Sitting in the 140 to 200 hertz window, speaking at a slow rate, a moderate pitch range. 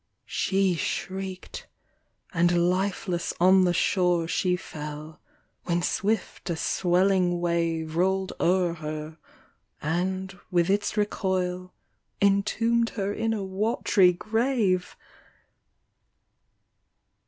No: medium, 185 Hz; slow, 95 wpm; narrow, 2.1 semitones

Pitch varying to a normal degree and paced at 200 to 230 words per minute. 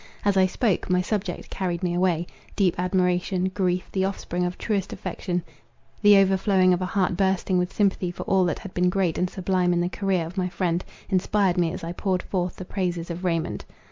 No: narrow, 1.4 semitones; fast, 205 wpm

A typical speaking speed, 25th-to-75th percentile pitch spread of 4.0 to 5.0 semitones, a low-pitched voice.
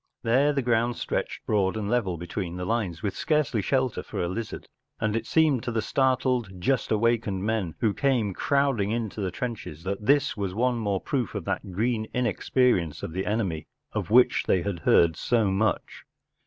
Yes: average, 185 wpm; average, 4.3 semitones; low, 110 Hz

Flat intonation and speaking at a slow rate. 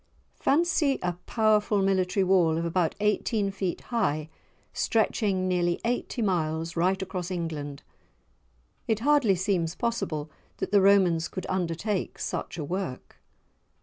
No: average, 3.8 semitones; slow, 125 wpm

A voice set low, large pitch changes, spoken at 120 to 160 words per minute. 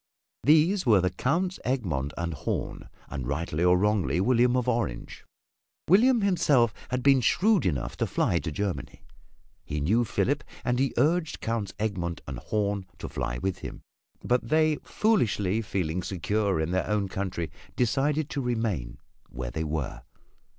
Yes: low, 105 Hz; wide, 7.5 semitones; average, 155 wpm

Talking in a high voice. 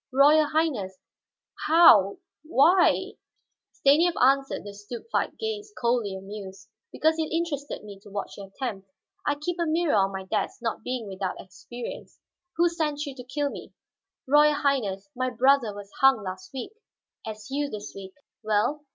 Yes: very high, 255 Hz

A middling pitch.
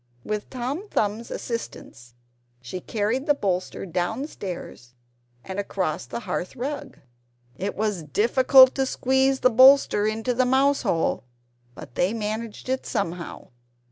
No: high, 220 Hz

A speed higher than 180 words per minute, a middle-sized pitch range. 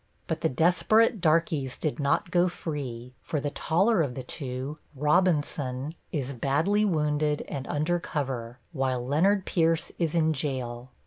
No: average, 145 wpm; average, 4.2 semitones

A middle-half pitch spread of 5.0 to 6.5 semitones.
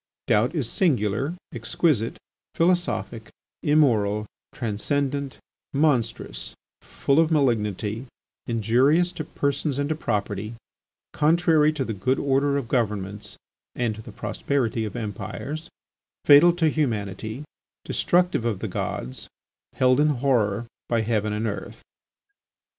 Yes: wide, 5.5 semitones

